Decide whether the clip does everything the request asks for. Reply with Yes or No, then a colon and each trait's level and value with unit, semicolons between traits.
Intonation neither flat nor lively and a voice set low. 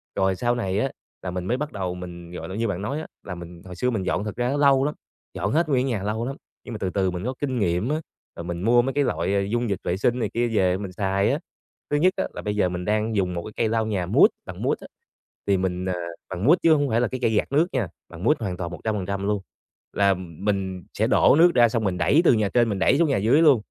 Yes: average, 5.0 semitones; low, 105 Hz